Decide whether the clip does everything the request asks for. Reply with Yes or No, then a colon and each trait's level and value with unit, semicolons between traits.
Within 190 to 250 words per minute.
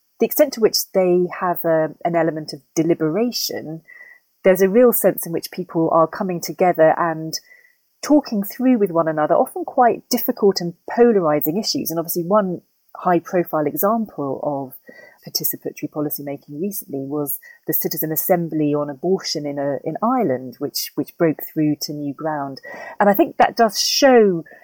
No: average, 160 wpm